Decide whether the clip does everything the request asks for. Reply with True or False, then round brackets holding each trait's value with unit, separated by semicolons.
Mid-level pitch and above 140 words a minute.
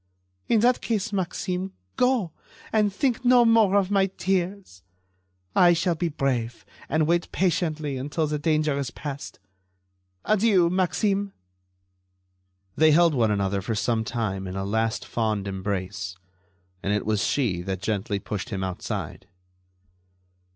False (150 Hz; 135 wpm)